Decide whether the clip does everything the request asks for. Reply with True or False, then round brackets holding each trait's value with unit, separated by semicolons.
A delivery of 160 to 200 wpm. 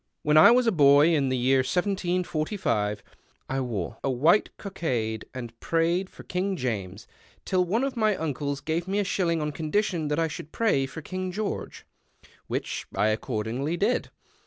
True (170 wpm)